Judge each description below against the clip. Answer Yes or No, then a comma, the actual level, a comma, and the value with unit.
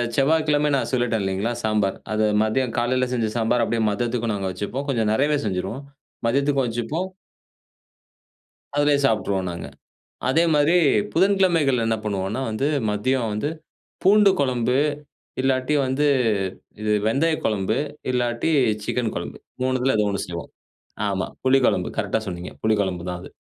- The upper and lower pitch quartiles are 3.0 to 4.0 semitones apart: No, average, 4.4 semitones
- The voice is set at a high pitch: No, low, 120 Hz